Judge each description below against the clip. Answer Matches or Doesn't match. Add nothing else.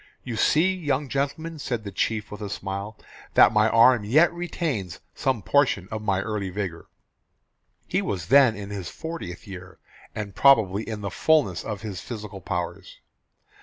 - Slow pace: Doesn't match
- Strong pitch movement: Matches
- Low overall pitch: Matches